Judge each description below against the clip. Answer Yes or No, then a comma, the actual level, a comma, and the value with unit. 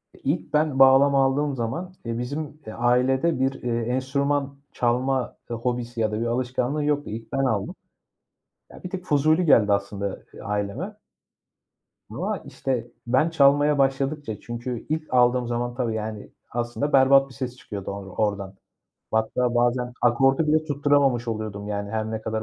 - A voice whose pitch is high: No, low, 125 Hz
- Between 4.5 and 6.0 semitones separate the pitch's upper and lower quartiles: No, average, 3.5 semitones